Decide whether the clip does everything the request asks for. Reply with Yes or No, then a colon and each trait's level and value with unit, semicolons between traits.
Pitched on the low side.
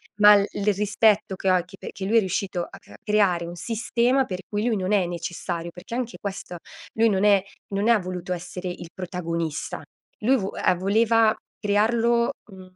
No: high, 200 Hz